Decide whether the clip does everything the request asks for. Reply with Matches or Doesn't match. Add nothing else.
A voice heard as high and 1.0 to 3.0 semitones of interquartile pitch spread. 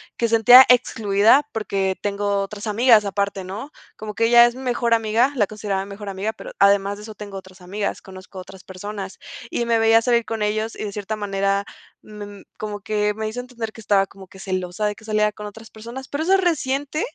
Matches